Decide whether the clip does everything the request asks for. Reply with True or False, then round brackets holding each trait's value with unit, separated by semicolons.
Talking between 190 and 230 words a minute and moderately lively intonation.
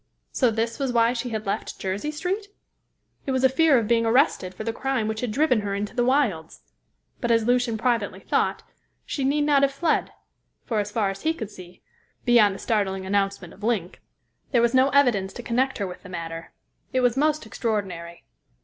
True (205 wpm; 4.7 semitones)